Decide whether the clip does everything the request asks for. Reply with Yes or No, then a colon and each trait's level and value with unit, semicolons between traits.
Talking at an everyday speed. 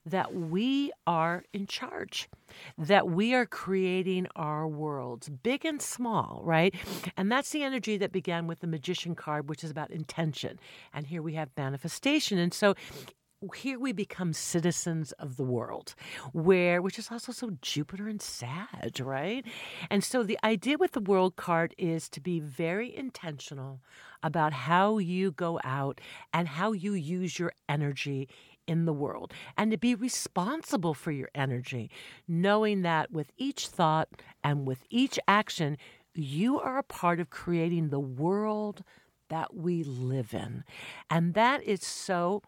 Yes: average, 155 wpm